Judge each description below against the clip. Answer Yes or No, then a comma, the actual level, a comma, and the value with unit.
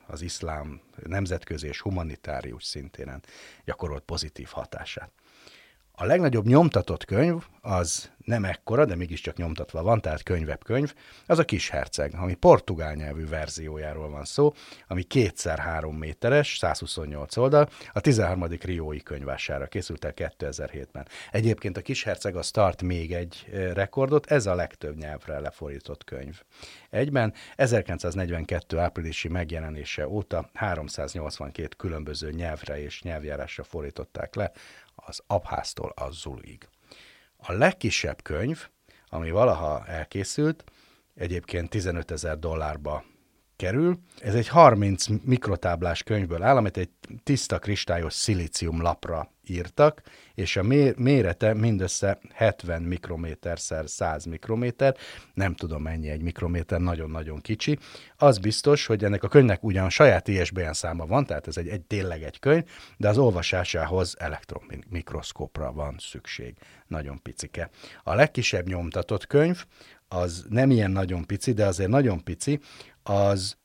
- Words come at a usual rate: Yes, average, 130 wpm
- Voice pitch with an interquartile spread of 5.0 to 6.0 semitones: Yes, wide, 5.4 semitones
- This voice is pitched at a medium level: No, very low, 90 Hz